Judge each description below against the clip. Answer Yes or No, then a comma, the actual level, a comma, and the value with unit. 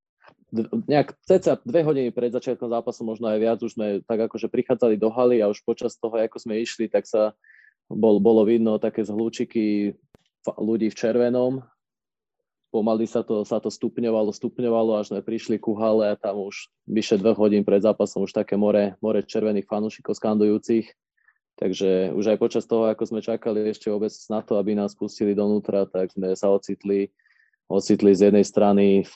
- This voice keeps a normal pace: No, fast, 180 wpm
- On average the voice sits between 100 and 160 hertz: Yes, low, 110 Hz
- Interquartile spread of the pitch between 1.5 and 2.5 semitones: Yes, narrow, 1.8 semitones